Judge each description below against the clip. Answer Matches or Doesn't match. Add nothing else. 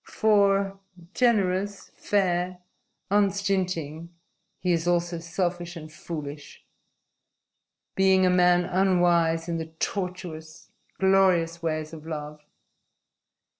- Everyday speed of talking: Doesn't match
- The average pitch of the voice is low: Doesn't match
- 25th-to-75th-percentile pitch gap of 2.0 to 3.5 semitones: Matches